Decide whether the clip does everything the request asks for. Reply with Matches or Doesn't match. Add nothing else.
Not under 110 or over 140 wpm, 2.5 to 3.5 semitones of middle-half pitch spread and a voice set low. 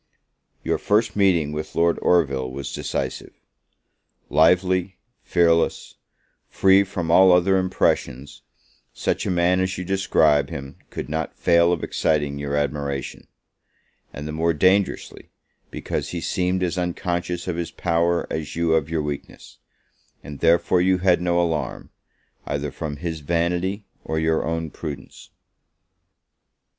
Matches